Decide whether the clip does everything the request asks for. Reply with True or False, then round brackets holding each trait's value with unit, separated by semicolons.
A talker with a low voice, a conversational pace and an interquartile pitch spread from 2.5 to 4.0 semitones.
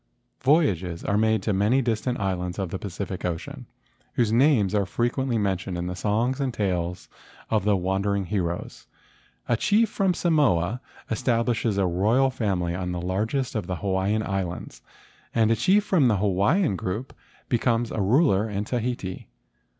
False (105 Hz; 160 wpm; 4.5 semitones)